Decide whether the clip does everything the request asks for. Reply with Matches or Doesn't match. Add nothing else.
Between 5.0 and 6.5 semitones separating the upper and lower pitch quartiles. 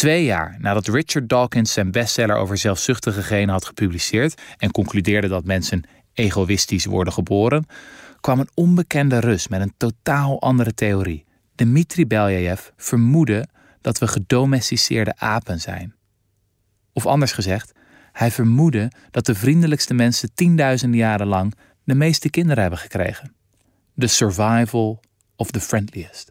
Doesn't match